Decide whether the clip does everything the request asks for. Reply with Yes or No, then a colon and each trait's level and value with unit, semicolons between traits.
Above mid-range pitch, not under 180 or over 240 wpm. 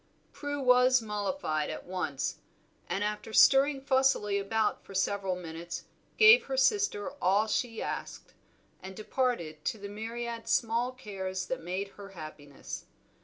No: high, 210 Hz; slow, 135 wpm